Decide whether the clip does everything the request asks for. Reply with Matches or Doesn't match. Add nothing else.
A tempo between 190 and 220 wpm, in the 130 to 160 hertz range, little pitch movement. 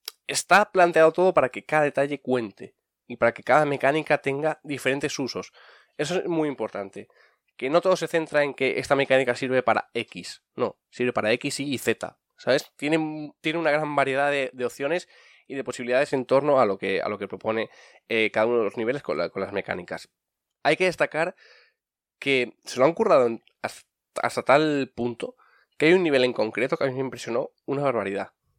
Doesn't match